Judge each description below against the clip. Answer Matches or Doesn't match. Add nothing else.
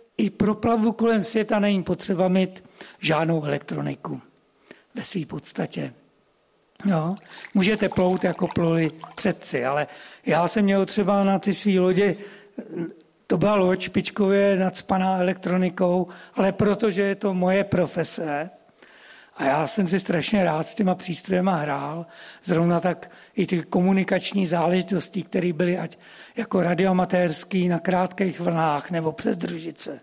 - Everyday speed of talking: Matches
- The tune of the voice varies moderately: Doesn't match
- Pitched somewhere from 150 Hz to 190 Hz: Matches